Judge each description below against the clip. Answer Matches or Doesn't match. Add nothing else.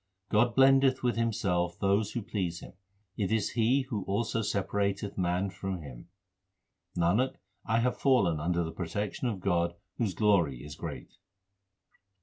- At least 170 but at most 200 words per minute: Doesn't match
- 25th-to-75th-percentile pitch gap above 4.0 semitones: Matches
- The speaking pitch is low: Matches